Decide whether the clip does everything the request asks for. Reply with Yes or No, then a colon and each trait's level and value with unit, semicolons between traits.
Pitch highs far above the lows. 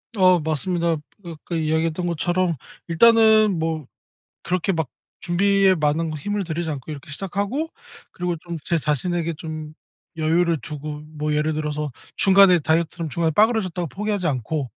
No: average, 3.0 semitones